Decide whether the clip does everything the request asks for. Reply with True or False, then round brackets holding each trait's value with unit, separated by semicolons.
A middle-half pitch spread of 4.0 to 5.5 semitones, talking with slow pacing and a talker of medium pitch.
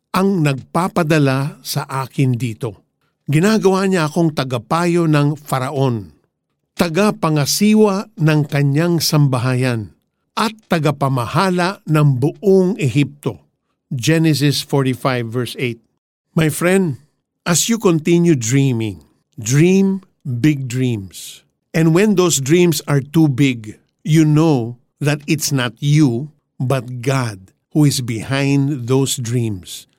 True (4.3 semitones; 105 wpm; 145 Hz)